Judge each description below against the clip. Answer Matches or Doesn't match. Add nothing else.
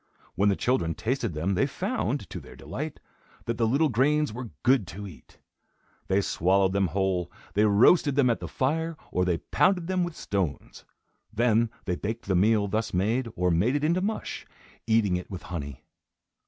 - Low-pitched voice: Matches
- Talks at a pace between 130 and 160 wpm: Doesn't match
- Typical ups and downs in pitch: Doesn't match